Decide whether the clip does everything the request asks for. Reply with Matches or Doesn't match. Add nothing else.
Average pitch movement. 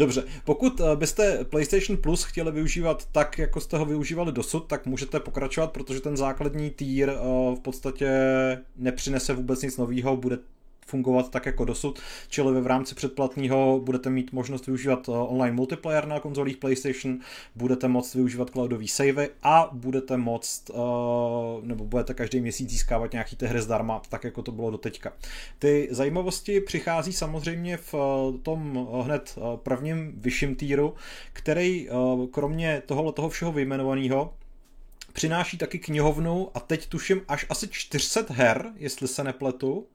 Matches